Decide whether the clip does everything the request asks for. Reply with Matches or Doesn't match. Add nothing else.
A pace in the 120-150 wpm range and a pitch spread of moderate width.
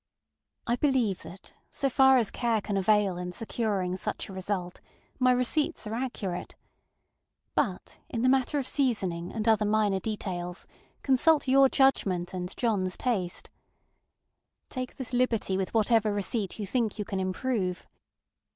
Matches